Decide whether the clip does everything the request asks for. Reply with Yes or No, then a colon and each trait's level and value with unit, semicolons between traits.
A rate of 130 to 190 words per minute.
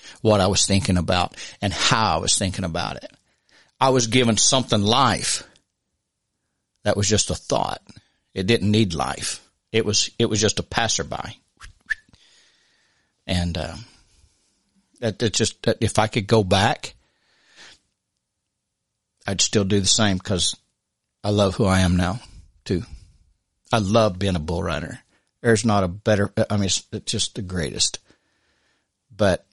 Yes: average, 150 wpm